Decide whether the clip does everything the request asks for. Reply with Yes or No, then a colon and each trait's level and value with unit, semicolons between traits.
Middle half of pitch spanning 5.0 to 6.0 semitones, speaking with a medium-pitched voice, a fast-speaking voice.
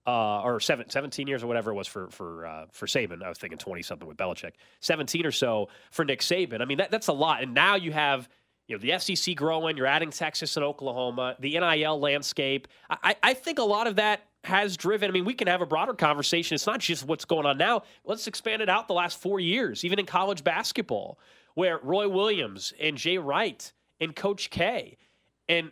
Yes: average, 5.3 semitones; medium, 165 Hz; fast, 225 wpm